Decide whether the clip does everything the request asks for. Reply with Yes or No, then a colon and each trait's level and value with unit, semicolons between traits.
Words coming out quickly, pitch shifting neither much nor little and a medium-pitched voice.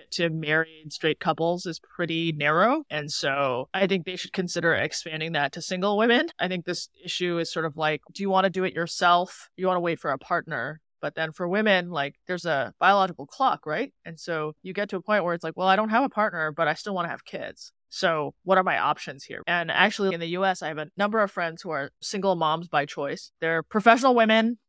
Yes: fast, 245 wpm; average, 3.1 semitones; medium, 175 Hz